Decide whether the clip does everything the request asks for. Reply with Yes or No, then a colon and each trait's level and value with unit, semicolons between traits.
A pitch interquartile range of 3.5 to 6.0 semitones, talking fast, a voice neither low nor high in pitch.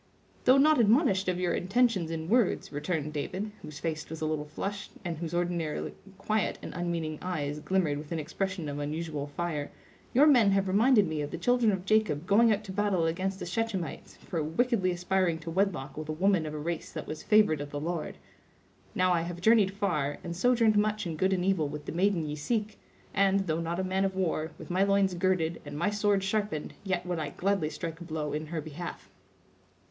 Yes: average, 4.1 semitones; fast, 215 wpm; medium, 180 Hz